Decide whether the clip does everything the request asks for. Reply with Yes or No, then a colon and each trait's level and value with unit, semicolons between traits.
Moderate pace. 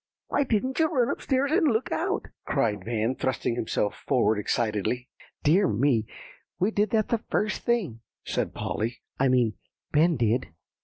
Yes: average, 160 wpm